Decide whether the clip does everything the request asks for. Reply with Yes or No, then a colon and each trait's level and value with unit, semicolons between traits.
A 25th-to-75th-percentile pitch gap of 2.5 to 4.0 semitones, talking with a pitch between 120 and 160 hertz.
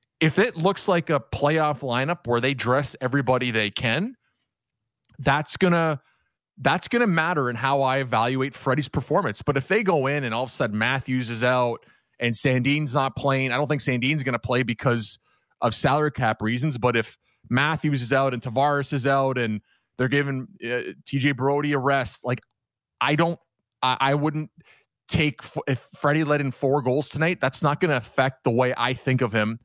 Yes: average, 3.1 semitones; low, 135 Hz